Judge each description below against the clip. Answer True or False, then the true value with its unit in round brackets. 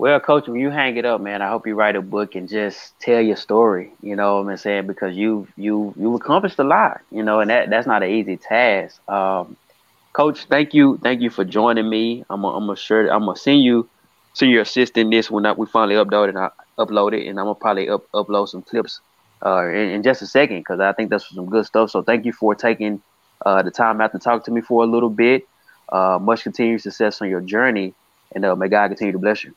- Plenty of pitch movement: False (2.6 semitones)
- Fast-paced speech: True (240 wpm)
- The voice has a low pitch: True (110 Hz)